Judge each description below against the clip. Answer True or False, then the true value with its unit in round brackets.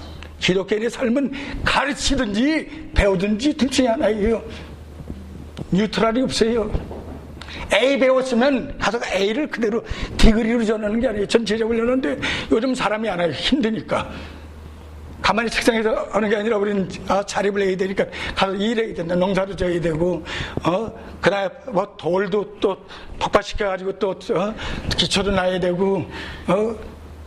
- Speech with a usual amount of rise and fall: True (4.5 semitones)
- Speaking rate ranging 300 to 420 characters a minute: True (305 characters per minute)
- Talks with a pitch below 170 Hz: False (205 Hz)